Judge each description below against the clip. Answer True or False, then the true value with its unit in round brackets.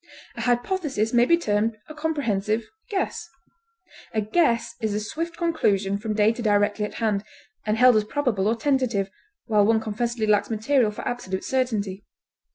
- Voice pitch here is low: False (225 Hz)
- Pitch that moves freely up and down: False (3.5 semitones)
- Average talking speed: True (160 wpm)